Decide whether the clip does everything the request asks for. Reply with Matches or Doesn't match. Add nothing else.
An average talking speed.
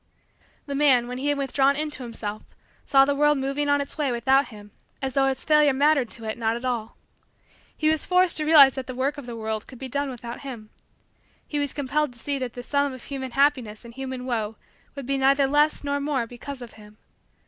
Doesn't match